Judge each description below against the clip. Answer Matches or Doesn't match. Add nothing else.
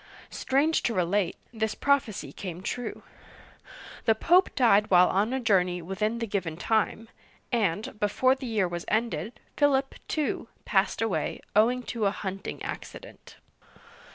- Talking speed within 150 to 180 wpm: Doesn't match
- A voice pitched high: Matches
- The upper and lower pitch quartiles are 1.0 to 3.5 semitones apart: Doesn't match